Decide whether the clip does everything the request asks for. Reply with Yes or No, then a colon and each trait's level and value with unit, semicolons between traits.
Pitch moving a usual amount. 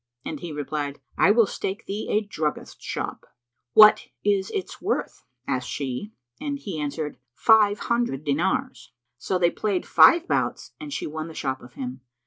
No: wide, 6.6 semitones